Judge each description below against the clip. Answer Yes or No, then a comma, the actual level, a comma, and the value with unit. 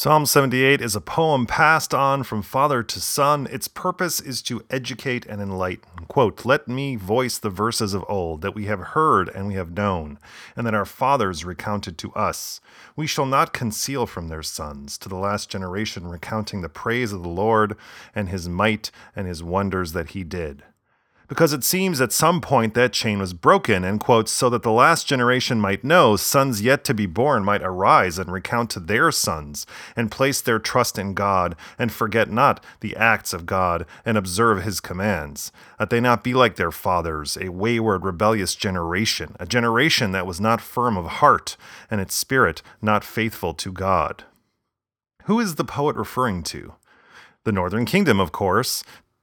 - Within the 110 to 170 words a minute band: No, average, 185 wpm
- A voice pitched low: Yes, low, 105 Hz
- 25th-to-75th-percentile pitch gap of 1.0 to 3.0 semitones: No, average, 4.7 semitones